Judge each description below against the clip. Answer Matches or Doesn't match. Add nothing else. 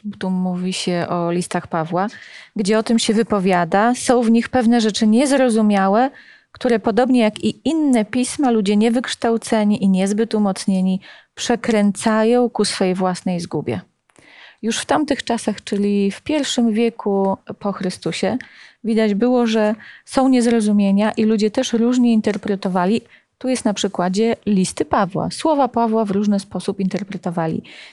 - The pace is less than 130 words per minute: Doesn't match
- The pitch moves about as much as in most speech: Matches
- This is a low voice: Doesn't match